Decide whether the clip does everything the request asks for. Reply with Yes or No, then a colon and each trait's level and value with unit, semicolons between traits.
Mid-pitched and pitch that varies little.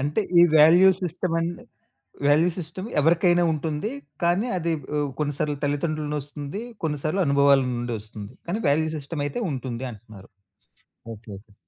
No: medium, 150 Hz; average, 3.7 semitones